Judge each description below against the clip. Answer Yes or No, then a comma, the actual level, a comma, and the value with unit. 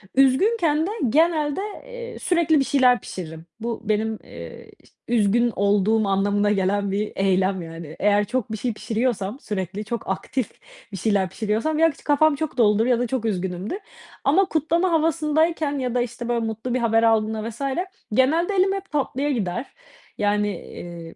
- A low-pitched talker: No, high, 230 Hz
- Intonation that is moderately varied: No, wide, 6.3 semitones